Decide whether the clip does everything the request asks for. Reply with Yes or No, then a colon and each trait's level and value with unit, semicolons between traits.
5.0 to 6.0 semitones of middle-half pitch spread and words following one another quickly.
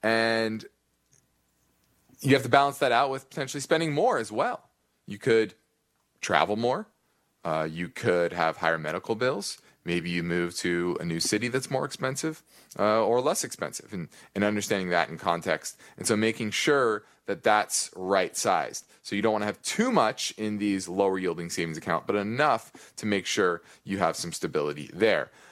No: wide, 5.6 semitones; average, 180 wpm